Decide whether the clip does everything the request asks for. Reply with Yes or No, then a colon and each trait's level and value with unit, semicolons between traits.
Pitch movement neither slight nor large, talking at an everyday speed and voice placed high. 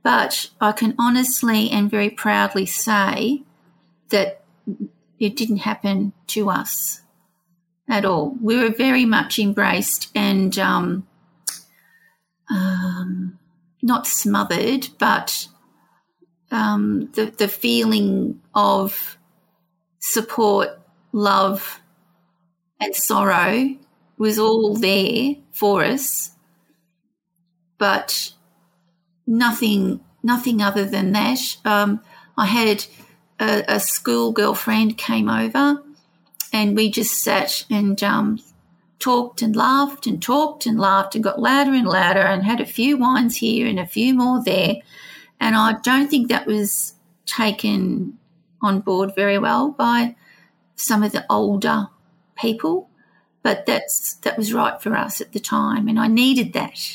No: average, 4.1 semitones; slow, 120 wpm; high, 210 Hz